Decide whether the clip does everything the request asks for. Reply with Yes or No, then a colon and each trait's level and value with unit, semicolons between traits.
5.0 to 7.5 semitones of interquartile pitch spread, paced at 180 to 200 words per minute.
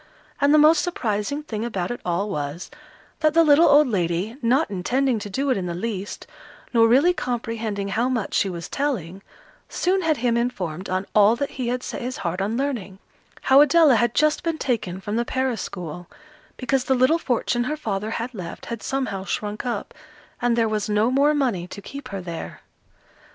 Yes: wide, 5.5 semitones; average, 195 wpm